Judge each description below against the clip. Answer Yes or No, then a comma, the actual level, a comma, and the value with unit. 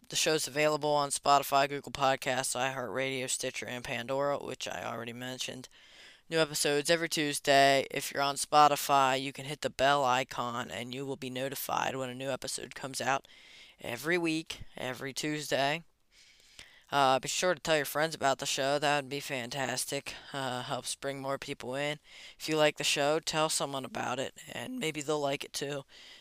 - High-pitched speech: No, medium, 140 Hz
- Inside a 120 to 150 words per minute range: No, average, 180 wpm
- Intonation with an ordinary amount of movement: No, narrow, 2.2 semitones